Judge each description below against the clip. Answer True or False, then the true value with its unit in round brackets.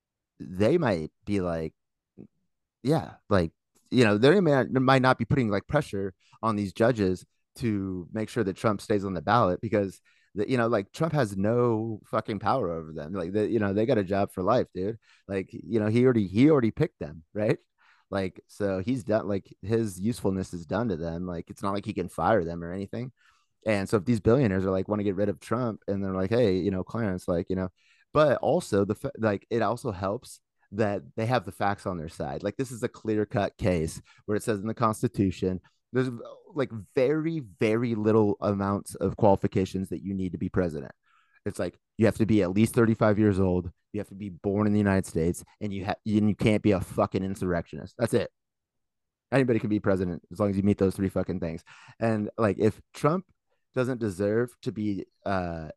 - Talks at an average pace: False (215 wpm)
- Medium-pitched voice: False (105 Hz)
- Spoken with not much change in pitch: False (3.2 semitones)